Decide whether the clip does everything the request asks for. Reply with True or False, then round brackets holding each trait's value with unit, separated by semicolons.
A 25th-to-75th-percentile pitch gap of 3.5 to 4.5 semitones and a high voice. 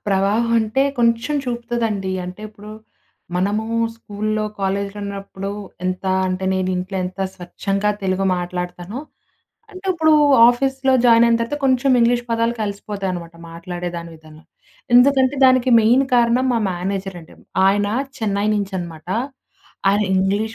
True (3.9 semitones; 205 Hz)